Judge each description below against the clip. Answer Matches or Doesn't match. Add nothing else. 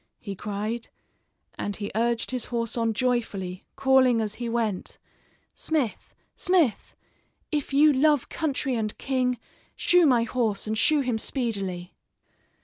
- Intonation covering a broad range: Doesn't match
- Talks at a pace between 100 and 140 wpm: Matches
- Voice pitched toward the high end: Matches